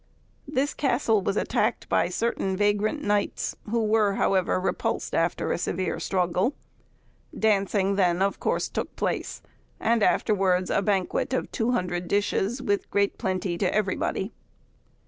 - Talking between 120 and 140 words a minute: Yes, slow, 135 wpm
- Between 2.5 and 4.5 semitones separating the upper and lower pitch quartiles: Yes, average, 2.8 semitones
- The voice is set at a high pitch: Yes, high, 200 Hz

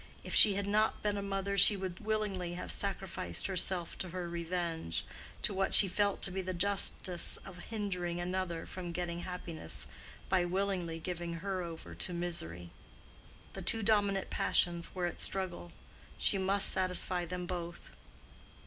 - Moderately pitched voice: Yes, medium, 180 Hz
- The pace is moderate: Yes, average, 155 wpm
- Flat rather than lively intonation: Yes, narrow, 2.2 semitones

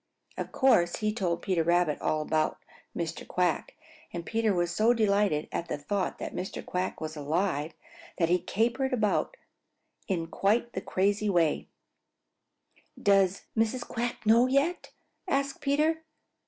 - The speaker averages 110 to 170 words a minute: Yes, average, 140 wpm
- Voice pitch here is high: Yes, high, 195 Hz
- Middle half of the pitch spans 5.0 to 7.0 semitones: Yes, average, 5.3 semitones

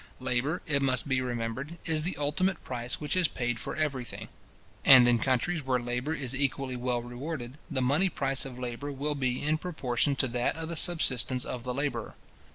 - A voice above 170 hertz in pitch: No, low, 135 Hz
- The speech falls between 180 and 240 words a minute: Yes, average, 195 wpm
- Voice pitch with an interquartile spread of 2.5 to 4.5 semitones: Yes, average, 3.3 semitones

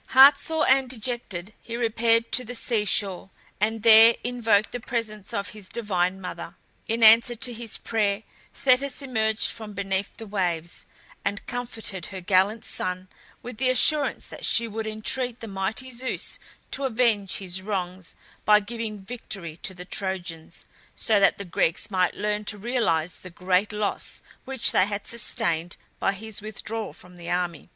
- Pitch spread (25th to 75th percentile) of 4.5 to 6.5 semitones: No, average, 3.5 semitones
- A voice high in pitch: Yes, high, 215 Hz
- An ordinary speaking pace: Yes, average, 165 wpm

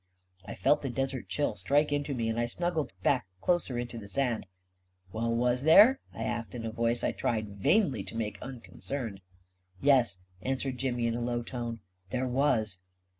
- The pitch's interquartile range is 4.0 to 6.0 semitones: No, average, 3.1 semitones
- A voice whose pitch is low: Yes, low, 120 Hz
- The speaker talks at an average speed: Yes, average, 190 wpm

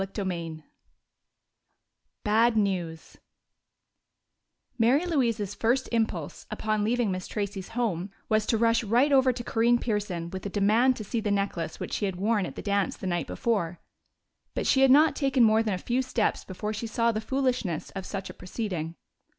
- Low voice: No, high, 215 Hz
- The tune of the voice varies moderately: Yes, average, 3.8 semitones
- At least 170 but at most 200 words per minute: Yes, average, 175 wpm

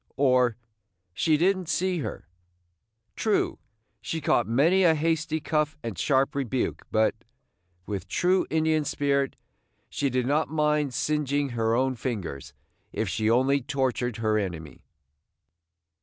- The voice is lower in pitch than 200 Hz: Yes, medium, 140 Hz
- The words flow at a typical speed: No, slow, 130 wpm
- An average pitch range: Yes, average, 4.8 semitones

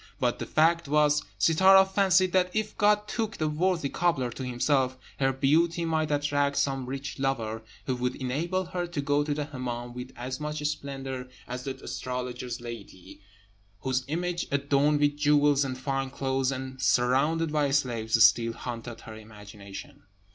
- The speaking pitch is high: No, medium, 140 Hz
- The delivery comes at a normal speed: Yes, average, 160 wpm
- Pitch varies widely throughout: No, average, 3.5 semitones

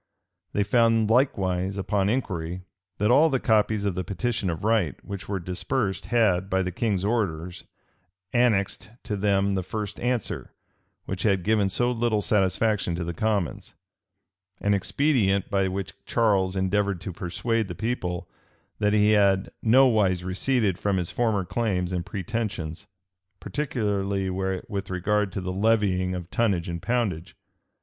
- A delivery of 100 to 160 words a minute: Yes, average, 145 wpm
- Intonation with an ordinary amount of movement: Yes, average, 3.1 semitones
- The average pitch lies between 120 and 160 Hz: No, low, 100 Hz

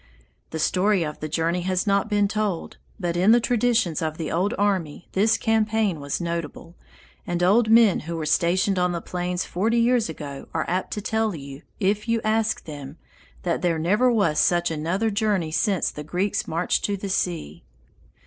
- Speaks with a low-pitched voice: No, medium, 185 Hz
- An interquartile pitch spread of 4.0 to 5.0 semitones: Yes, average, 4.4 semitones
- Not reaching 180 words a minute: No, average, 185 wpm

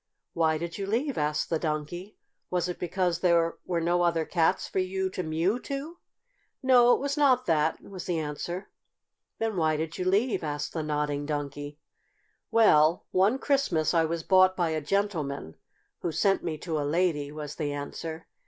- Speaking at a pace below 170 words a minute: No, average, 180 wpm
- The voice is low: No, medium, 170 Hz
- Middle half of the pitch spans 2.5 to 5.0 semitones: Yes, average, 3.7 semitones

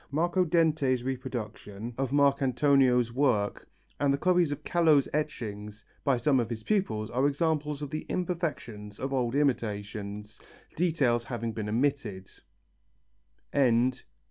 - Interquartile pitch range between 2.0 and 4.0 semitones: No, average, 4.8 semitones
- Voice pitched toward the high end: No, low, 135 Hz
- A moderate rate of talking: No, slow, 120 wpm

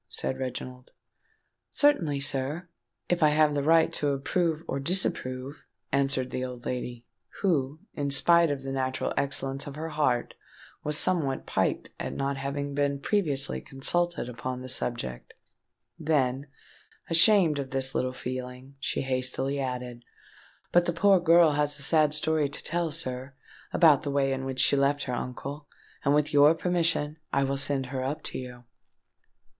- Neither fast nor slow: Yes, average, 160 wpm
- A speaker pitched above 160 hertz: No, medium, 140 Hz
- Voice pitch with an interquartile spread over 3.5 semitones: No, average, 2.9 semitones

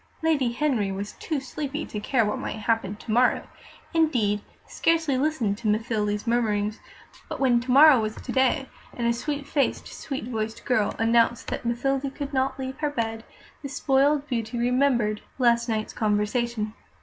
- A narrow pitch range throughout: No, average, 4.0 semitones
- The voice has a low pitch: No, high, 240 Hz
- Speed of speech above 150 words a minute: Yes, average, 165 wpm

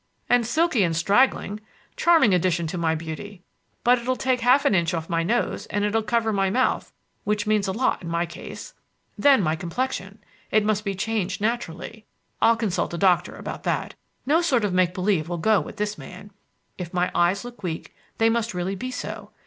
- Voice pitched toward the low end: No, high, 205 Hz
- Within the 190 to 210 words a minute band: Yes, average, 195 wpm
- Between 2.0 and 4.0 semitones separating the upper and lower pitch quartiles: No, average, 4.7 semitones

